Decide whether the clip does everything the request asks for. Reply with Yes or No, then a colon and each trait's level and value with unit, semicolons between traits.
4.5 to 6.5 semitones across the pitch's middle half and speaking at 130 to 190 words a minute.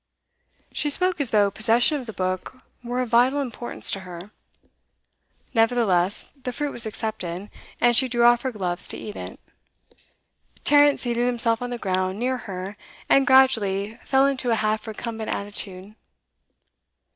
No: average, 3.8 semitones; average, 155 wpm